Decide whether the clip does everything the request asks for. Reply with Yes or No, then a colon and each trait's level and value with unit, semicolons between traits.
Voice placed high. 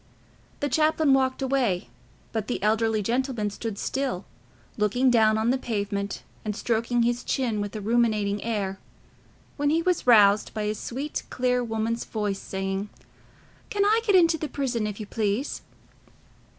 Yes: high, 230 Hz